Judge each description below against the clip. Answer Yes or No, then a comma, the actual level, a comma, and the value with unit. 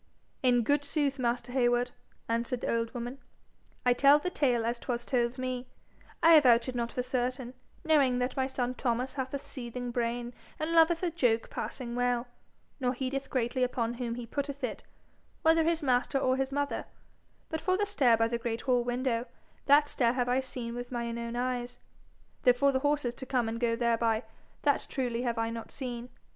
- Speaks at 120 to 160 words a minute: No, average, 195 wpm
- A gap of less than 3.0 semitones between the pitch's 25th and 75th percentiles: Yes, narrow, 2.4 semitones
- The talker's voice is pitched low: No, very high, 250 Hz